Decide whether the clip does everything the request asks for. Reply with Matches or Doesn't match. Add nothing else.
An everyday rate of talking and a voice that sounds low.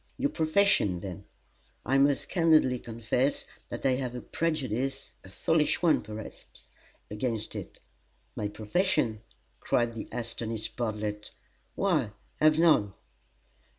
Doesn't match